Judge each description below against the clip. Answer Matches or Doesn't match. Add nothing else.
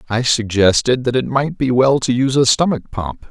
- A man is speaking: Matches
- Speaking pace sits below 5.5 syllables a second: Matches